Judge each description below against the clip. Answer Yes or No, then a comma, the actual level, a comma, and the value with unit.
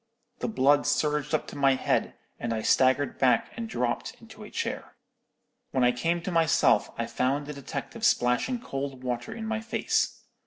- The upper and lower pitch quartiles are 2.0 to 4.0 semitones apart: No, average, 4.5 semitones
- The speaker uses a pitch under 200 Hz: Yes, medium, 140 Hz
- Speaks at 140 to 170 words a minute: No, average, 180 wpm